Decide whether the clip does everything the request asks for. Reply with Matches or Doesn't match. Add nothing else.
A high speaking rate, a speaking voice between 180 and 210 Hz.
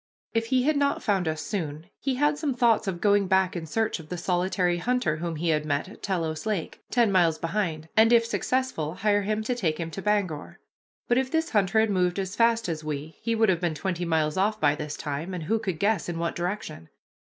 Matches